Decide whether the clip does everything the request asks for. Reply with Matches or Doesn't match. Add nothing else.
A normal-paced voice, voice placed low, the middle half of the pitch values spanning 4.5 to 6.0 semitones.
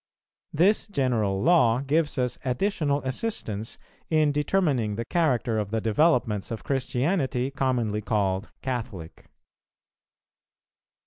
Doesn't match